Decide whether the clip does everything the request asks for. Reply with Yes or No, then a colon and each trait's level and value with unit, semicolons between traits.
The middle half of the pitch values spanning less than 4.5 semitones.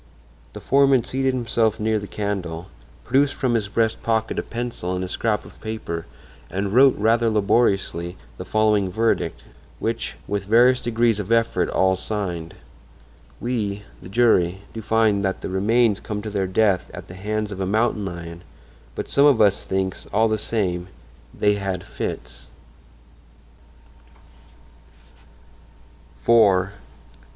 Yes: average, 3.2 semitones